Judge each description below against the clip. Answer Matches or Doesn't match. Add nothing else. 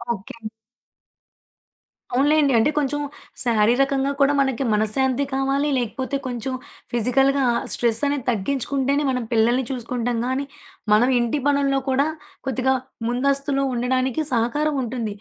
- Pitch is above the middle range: Matches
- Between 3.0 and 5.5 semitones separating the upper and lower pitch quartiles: Doesn't match